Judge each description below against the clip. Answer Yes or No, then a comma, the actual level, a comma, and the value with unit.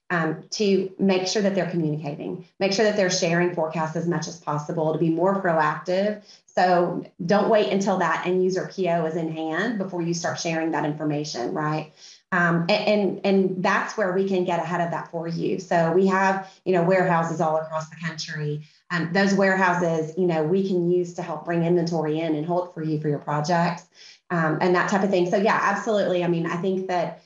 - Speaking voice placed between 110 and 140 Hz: No, medium, 175 Hz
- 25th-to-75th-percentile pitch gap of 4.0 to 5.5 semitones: No, average, 2.7 semitones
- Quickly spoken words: Yes, fast, 215 wpm